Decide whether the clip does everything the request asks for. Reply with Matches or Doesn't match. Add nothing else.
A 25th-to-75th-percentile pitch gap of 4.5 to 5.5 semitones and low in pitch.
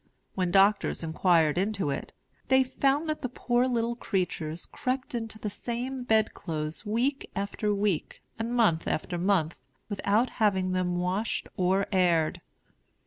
Doesn't match